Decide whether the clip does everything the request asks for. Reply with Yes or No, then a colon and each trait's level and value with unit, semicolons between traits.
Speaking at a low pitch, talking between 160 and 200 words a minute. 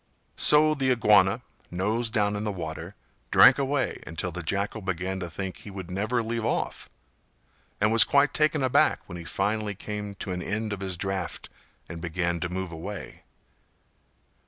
Yes: low, 100 Hz; average, 170 wpm